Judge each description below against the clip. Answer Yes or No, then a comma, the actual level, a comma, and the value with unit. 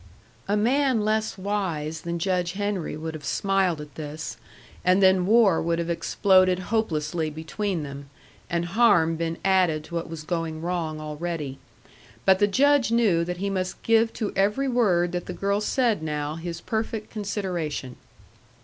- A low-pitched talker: No, medium, 180 Hz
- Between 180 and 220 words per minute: No, average, 160 wpm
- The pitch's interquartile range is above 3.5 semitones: Yes, average, 4.2 semitones